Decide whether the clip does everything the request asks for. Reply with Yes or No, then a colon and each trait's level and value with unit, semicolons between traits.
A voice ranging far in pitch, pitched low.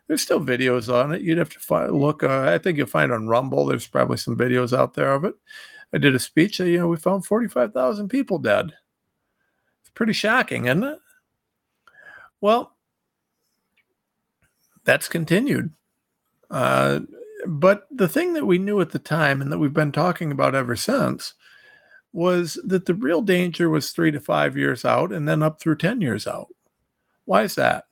No: wide, 7.2 semitones; medium, 170 Hz